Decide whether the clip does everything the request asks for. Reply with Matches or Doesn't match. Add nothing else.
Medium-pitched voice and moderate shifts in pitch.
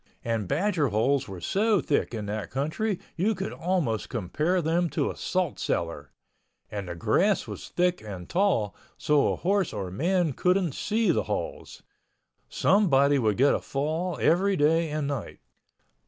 Doesn't match